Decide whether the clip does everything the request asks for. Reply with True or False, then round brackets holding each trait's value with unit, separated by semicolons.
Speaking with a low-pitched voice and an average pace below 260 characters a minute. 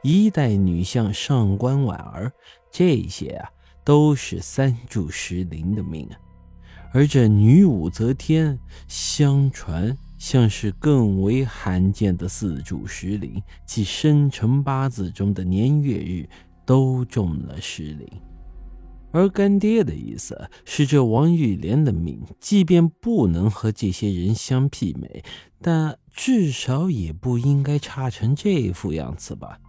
True (110 Hz; 185 characters per minute)